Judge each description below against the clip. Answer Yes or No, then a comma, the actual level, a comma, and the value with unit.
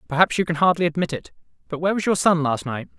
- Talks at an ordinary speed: No, fast, 260 wpm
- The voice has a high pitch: No, medium, 165 Hz